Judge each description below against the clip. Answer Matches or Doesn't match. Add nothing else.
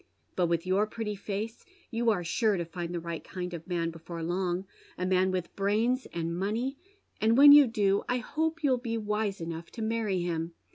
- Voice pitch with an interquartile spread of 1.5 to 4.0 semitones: Doesn't match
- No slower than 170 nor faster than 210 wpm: Matches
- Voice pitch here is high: Matches